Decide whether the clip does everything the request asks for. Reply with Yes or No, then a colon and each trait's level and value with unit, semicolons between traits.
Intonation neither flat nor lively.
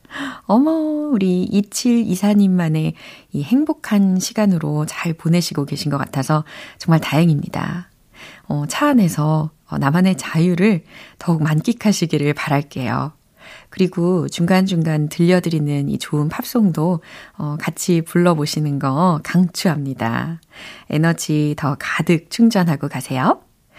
Yes: average, 4.2 semitones